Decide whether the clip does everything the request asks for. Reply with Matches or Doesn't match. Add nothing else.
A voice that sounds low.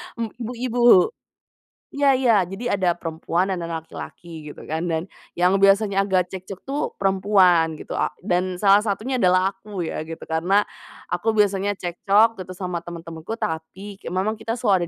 Doesn't match